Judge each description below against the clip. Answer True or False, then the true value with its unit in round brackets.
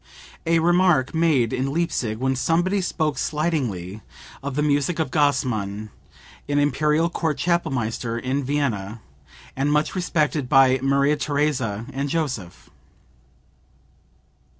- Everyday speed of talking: False (115 wpm)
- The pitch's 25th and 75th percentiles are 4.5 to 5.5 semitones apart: False (3.8 semitones)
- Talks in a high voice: False (140 Hz)